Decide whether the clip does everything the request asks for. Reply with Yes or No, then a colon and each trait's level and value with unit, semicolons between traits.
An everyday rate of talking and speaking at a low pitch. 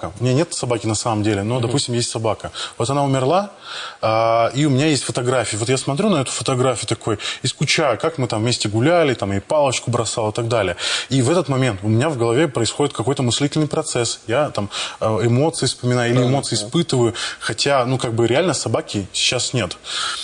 No: fast, 200 wpm; low, 125 Hz